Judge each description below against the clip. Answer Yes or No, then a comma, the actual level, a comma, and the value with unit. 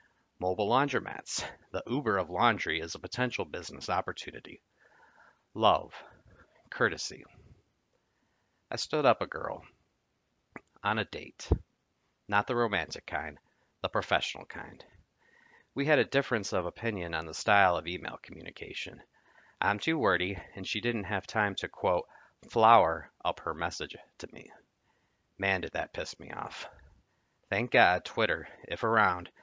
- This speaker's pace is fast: No, slow, 135 wpm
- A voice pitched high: No, low, 100 Hz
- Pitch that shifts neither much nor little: Yes, average, 4.8 semitones